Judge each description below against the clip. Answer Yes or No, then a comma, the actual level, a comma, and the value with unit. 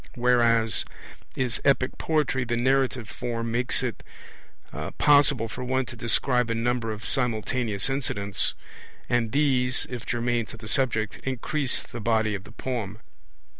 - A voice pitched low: Yes, low, 120 Hz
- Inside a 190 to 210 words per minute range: No, average, 140 wpm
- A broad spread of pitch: No, narrow, 2.4 semitones